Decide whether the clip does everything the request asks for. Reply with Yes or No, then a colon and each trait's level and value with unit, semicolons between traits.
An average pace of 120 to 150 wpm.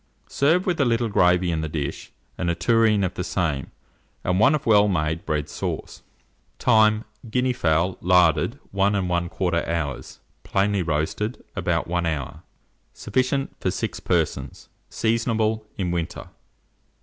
Yes: average, 140 wpm